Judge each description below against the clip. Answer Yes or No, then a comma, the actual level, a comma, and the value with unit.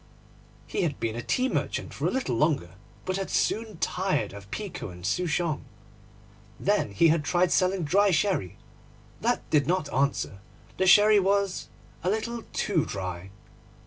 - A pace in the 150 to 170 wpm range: Yes, average, 155 wpm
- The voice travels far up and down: Yes, wide, 8.7 semitones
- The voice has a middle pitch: Yes, medium, 175 Hz